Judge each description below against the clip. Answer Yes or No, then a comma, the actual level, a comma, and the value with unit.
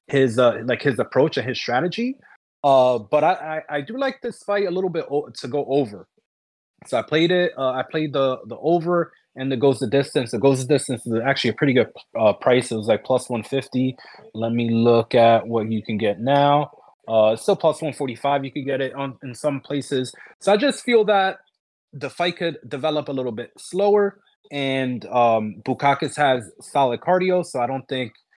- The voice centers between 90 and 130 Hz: No, medium, 140 Hz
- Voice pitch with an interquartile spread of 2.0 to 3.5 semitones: No, average, 4.2 semitones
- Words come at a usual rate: No, fast, 210 wpm